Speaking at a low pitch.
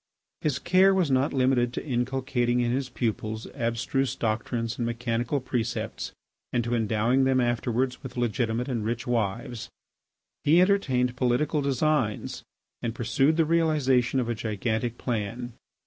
Yes: low, 125 Hz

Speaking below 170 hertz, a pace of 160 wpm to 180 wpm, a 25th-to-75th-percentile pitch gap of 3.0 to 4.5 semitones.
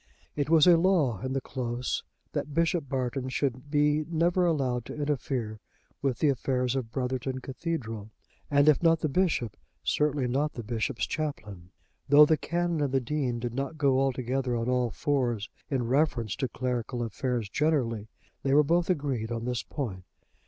Yes: low, 135 Hz; average, 170 wpm; average, 3.6 semitones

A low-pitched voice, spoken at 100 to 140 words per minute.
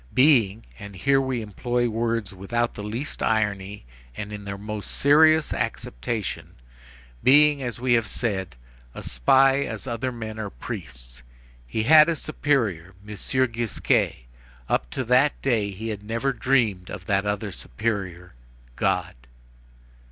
Yes: low, 110 Hz; slow, 135 wpm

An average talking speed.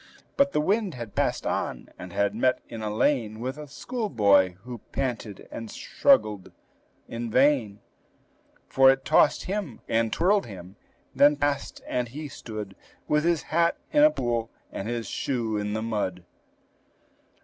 Yes: average, 155 wpm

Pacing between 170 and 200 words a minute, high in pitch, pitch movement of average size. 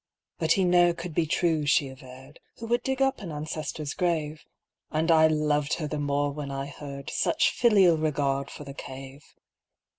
No: average, 185 wpm; medium, 150 Hz; average, 3.2 semitones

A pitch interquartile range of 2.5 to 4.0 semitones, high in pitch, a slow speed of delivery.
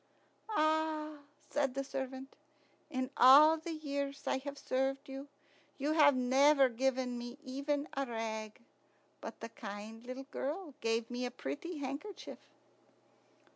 Yes: average, 2.8 semitones; very high, 270 Hz; slow, 130 wpm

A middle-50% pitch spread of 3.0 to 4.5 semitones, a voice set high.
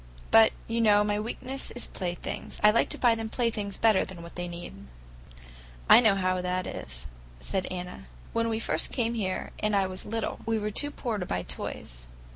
Yes: average, 3.7 semitones; high, 210 Hz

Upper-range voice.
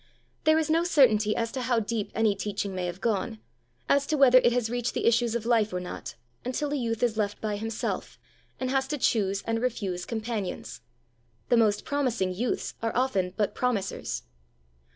Yes: high, 225 Hz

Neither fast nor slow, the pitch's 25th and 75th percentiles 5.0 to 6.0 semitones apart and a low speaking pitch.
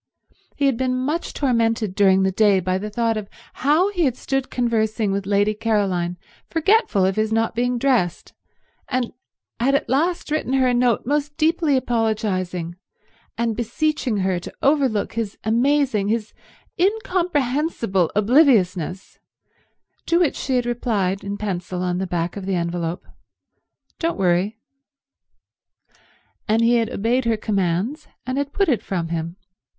No: average, 150 wpm; wide, 5.6 semitones; high, 225 Hz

